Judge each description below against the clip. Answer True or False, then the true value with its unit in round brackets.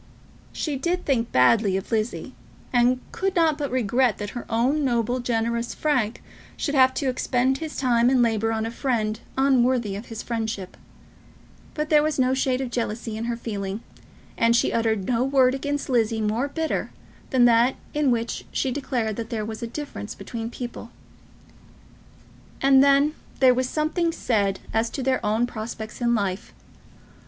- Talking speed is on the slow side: False (170 wpm)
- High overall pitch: True (240 Hz)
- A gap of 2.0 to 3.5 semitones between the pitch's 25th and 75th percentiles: True (3.0 semitones)